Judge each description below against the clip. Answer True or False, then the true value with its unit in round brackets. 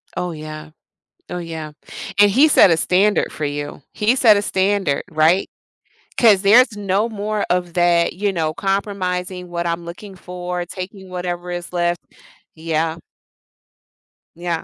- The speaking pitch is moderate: True (180 Hz)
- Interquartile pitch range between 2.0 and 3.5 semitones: True (2.9 semitones)